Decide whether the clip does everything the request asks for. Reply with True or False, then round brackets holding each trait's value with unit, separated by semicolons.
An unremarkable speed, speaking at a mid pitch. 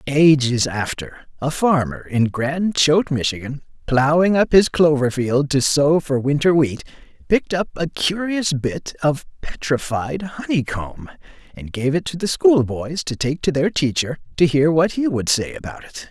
True (170 wpm; 145 Hz)